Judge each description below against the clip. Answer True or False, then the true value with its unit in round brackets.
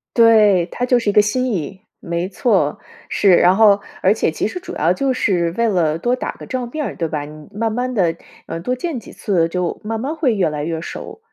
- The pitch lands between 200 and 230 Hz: True (205 Hz)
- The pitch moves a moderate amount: False (6.1 semitones)